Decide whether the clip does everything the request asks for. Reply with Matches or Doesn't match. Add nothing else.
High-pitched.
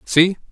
Doesn't match